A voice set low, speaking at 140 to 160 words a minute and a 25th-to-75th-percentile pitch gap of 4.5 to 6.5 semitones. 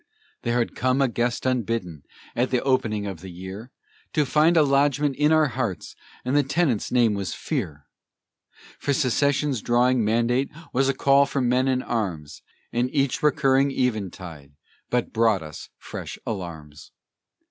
Yes: low, 125 Hz; average, 155 wpm; average, 5.0 semitones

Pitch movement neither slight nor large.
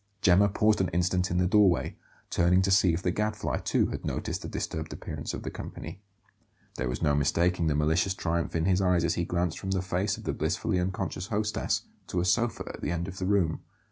No: narrow, 2.2 semitones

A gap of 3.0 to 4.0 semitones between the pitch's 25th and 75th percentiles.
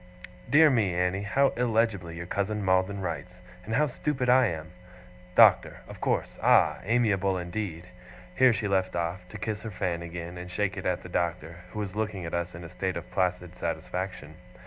Yes: average, 3.6 semitones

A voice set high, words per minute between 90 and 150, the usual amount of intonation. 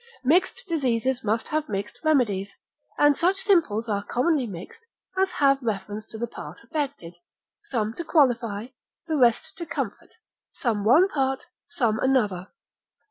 No: very high, 250 Hz; average, 140 wpm; wide, 6.3 semitones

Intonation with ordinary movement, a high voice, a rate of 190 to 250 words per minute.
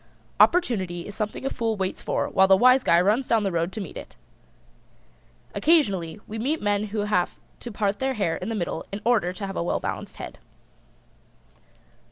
Yes: average, 3.5 semitones; high, 205 Hz; average, 195 wpm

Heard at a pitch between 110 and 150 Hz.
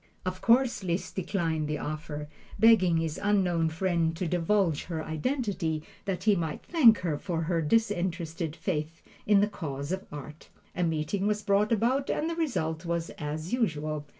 No: medium, 175 Hz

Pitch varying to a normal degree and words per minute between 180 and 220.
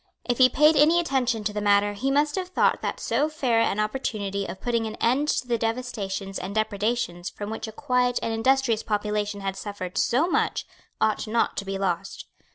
Yes: average, 3.9 semitones; average, 200 wpm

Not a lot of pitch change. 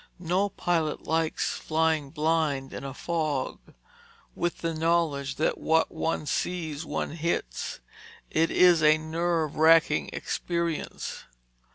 Yes: narrow, 1.8 semitones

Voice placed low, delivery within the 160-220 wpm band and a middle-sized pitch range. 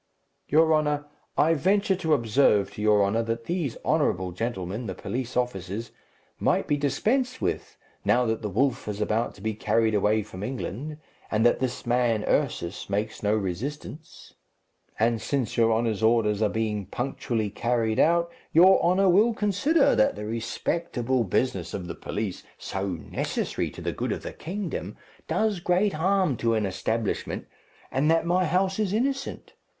No: low, 120 Hz; average, 165 wpm; wide, 7.4 semitones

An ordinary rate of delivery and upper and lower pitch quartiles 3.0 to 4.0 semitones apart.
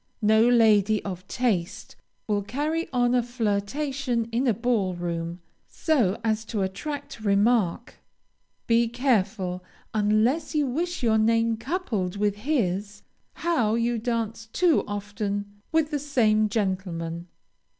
No: slow, 125 wpm; average, 3.6 semitones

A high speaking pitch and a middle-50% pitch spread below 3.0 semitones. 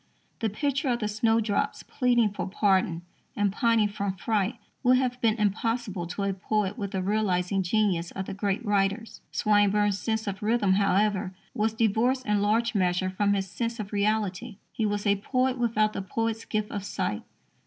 Yes: high, 210 Hz; narrow, 2.5 semitones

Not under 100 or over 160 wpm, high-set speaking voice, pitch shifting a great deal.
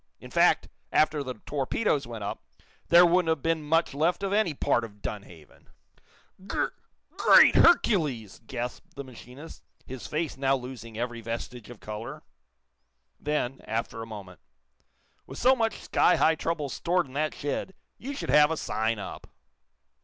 No: average, 155 wpm; medium, 140 Hz; wide, 5.7 semitones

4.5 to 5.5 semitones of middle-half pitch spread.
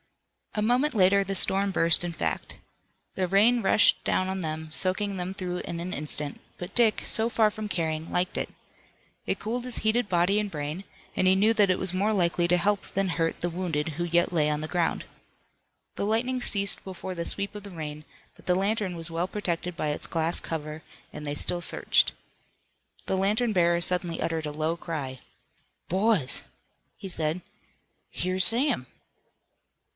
No: average, 3.4 semitones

